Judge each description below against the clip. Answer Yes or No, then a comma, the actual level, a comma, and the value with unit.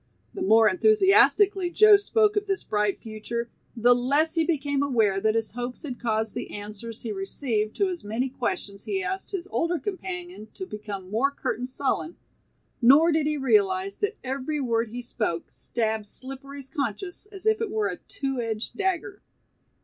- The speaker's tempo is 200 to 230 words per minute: No, average, 175 wpm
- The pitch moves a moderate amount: No, wide, 8.8 semitones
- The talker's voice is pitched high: Yes, very high, 275 Hz